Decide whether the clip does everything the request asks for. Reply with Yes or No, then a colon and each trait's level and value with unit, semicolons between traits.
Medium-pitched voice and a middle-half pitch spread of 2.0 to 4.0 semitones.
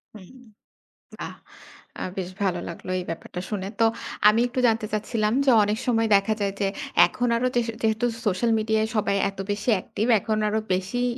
No: high, 215 Hz; narrow, 2.4 semitones